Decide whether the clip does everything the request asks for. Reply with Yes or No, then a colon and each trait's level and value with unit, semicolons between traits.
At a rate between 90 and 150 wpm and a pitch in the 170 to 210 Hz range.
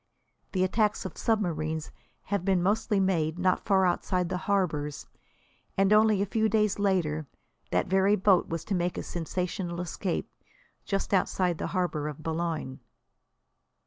Yes: average, 145 wpm; medium, 185 Hz